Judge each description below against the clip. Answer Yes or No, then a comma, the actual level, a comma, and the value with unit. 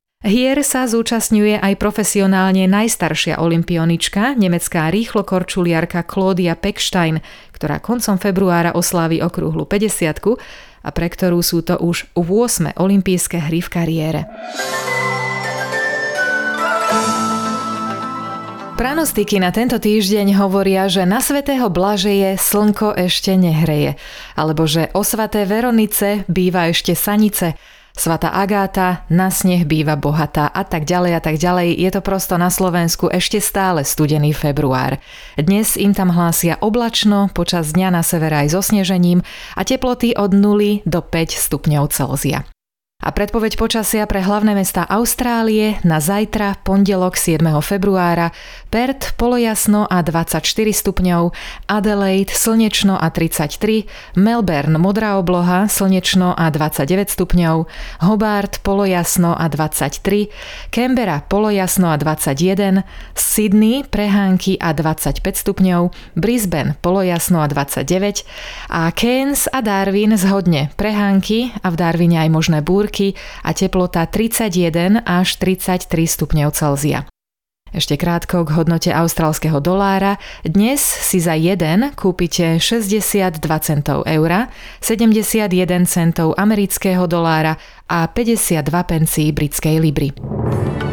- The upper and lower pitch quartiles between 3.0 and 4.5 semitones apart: Yes, average, 3.8 semitones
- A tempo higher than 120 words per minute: No, average, 115 wpm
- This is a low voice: No, medium, 185 Hz